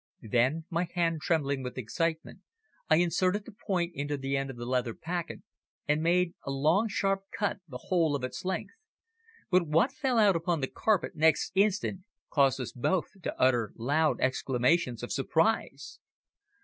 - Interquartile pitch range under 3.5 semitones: No, average, 5.2 semitones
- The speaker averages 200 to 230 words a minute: No, average, 165 wpm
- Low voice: No, medium, 160 Hz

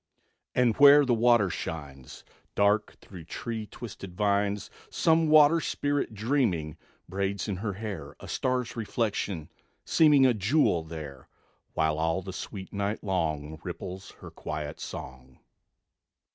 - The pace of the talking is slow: Yes, slow, 130 wpm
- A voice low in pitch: Yes, low, 100 Hz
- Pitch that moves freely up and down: Yes, wide, 6.6 semitones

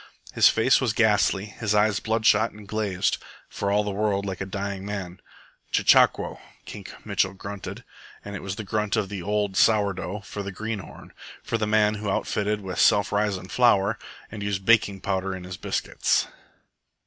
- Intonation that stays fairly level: Yes, narrow, 1.7 semitones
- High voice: No, low, 100 Hz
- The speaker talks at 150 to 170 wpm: No, average, 180 wpm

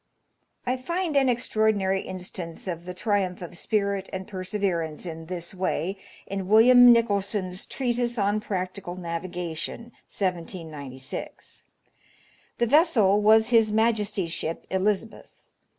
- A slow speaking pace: Yes, slow, 120 wpm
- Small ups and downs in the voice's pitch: No, average, 3.6 semitones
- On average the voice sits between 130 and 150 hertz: No, high, 195 Hz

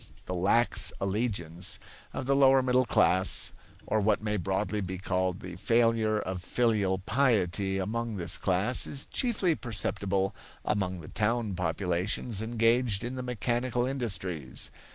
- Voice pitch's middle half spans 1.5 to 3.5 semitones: No, average, 4.2 semitones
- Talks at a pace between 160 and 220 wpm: No, slow, 135 wpm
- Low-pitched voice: Yes, low, 105 Hz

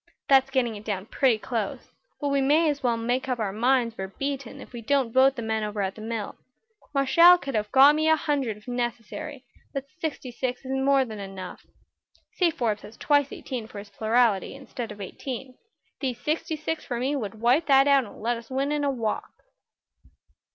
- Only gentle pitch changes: No, average, 3.9 semitones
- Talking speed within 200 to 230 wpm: Yes, fast, 205 wpm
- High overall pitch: Yes, very high, 255 Hz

